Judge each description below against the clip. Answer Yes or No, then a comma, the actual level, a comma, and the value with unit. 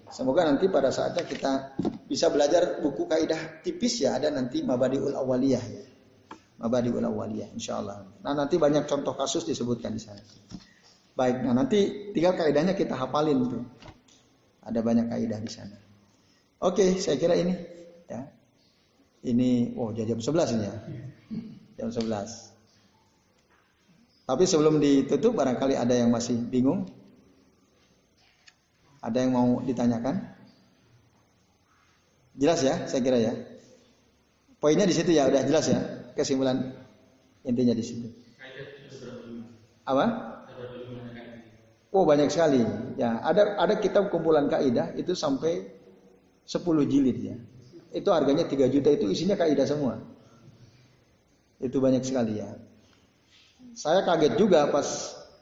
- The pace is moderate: Yes, average, 120 wpm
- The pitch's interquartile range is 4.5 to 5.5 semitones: Yes, average, 4.8 semitones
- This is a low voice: Yes, low, 130 Hz